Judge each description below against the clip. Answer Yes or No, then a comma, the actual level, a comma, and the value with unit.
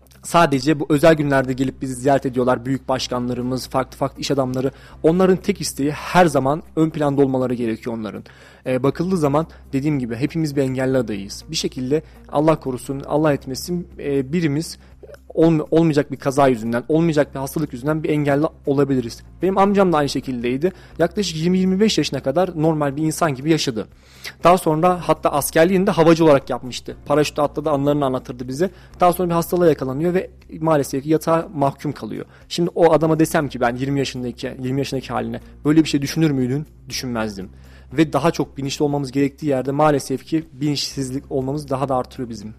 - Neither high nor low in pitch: Yes, medium, 145 Hz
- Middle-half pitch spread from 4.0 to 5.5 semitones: No, average, 3.5 semitones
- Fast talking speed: Yes, fast, 170 wpm